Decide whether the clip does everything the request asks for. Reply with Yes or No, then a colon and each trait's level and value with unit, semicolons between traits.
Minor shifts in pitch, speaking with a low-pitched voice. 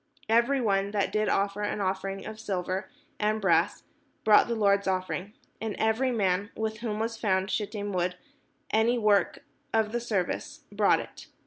No: narrow, 2.2 semitones; high, 210 Hz